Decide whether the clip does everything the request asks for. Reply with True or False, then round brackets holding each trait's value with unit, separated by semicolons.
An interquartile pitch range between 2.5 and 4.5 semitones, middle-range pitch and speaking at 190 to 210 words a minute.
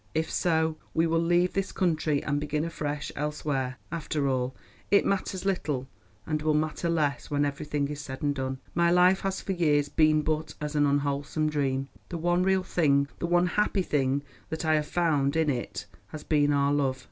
True (2.8 semitones; 150 Hz; 195 wpm)